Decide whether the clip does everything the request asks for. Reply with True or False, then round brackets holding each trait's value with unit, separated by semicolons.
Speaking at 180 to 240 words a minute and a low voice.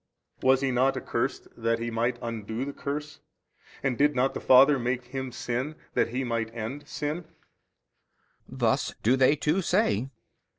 False (170 wpm; 130 Hz)